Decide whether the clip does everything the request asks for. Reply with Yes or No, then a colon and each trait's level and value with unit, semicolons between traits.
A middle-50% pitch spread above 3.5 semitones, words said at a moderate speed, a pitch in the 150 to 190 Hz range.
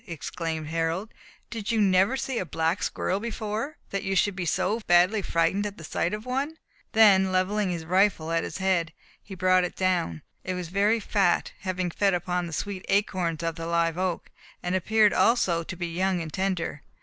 No: average, 3.2 semitones; average, 195 wpm; medium, 185 Hz